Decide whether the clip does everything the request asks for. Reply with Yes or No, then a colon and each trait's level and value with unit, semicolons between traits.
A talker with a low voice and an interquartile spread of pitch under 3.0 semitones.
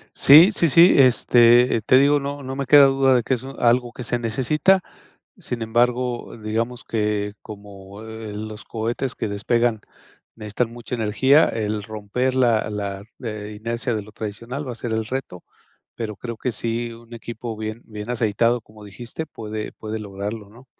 Yes: low, 115 Hz; narrow, 2.6 semitones